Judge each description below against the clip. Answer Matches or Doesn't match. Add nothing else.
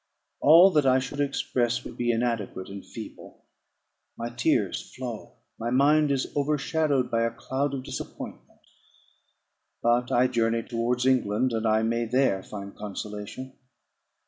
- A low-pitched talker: Matches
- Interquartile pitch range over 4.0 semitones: Doesn't match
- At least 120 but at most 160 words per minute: Matches